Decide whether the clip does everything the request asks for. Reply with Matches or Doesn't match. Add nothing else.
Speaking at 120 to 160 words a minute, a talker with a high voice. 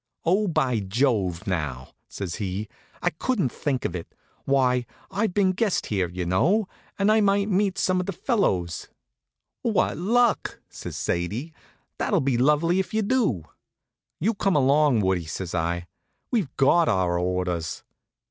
Doesn't match